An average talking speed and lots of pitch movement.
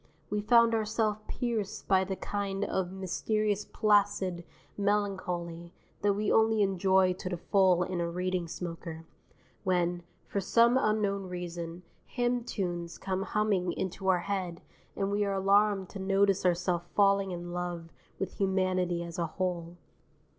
No: average, 145 wpm; narrow, 2.5 semitones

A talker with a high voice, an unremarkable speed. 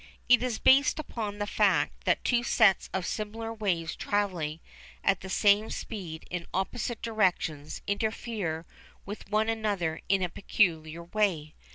Yes: high, 200 Hz; average, 145 wpm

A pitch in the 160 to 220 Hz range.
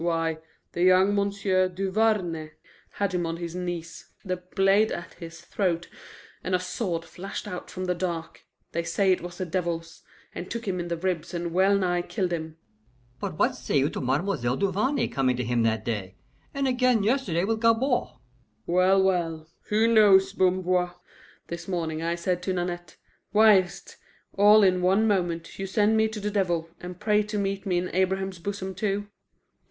Yes: medium, 185 Hz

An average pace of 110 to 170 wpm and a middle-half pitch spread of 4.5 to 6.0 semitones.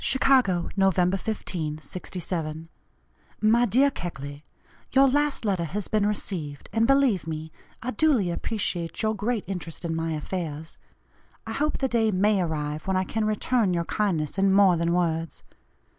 Yes: average, 155 wpm; average, 4.9 semitones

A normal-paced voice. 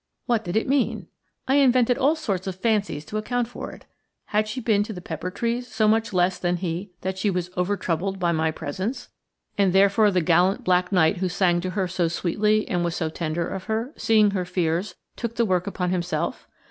No: fast, 215 wpm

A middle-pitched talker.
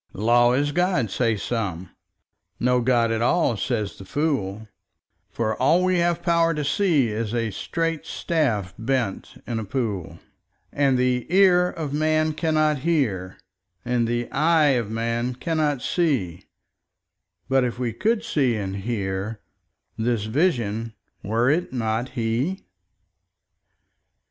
No: low, 125 Hz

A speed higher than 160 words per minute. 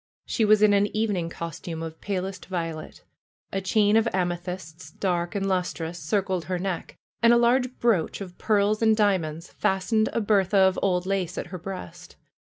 Yes: average, 170 wpm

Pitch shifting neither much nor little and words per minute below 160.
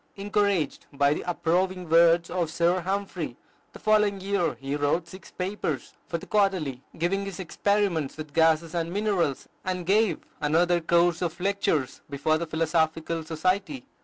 Yes: average, 3.5 semitones; average, 150 wpm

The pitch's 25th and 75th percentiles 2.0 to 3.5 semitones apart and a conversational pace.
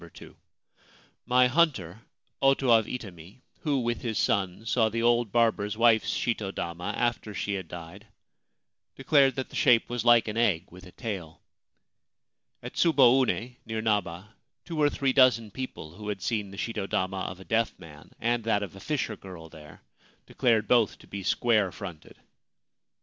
No: average, 4.0 semitones; average, 165 wpm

